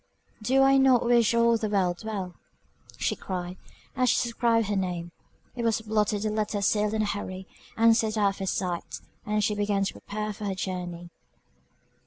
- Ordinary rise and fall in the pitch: Yes, average, 3.0 semitones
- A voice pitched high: Yes, high, 210 Hz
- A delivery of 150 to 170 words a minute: No, average, 190 wpm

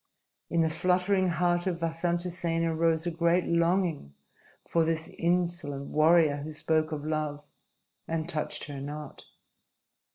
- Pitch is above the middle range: No, medium, 165 Hz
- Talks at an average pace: No, slow, 130 wpm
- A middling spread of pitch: No, narrow, 1.9 semitones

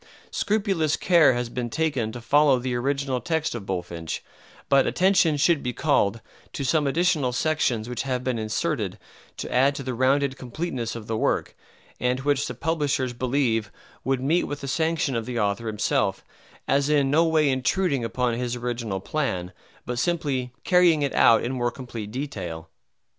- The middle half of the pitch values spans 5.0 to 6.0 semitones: No, average, 3.9 semitones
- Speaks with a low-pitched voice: Yes, low, 130 Hz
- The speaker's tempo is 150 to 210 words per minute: Yes, average, 170 wpm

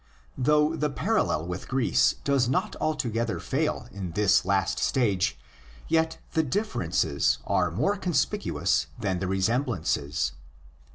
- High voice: No, low, 115 Hz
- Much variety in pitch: Yes, wide, 8.5 semitones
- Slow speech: Yes, slow, 120 wpm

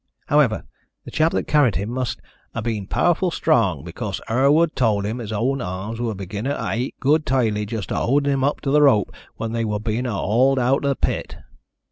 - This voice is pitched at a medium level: No, low, 120 Hz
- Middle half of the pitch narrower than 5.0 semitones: Yes, average, 4.3 semitones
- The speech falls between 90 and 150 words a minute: No, fast, 205 wpm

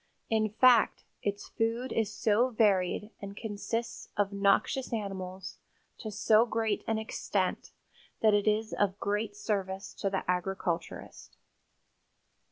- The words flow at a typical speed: No, slow, 125 wpm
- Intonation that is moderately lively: No, narrow, 2.1 semitones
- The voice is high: Yes, high, 205 Hz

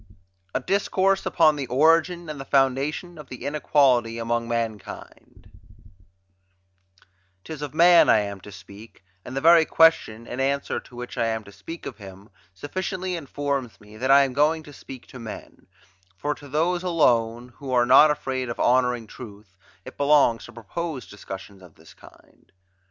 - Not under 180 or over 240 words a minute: No, average, 170 wpm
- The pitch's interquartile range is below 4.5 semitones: No, average, 5.0 semitones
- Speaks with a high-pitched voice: No, low, 130 Hz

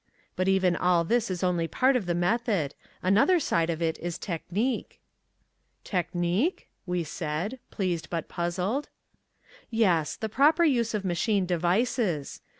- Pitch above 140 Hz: Yes, medium, 185 Hz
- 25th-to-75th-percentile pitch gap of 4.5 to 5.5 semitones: Yes, average, 4.8 semitones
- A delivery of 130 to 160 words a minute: Yes, average, 140 wpm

